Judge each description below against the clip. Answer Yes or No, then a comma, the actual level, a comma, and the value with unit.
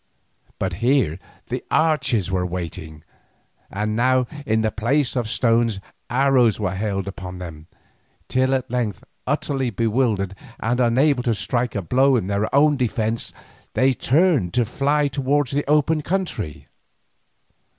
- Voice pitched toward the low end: Yes, low, 120 Hz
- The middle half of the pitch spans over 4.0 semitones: Yes, average, 5.1 semitones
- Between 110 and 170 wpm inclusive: Yes, average, 140 wpm